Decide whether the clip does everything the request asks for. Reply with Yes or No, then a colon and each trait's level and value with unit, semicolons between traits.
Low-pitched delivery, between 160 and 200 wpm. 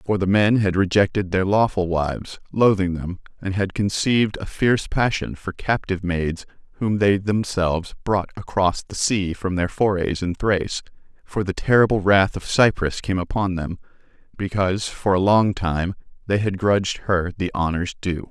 Yes: very low, 95 Hz; average, 170 wpm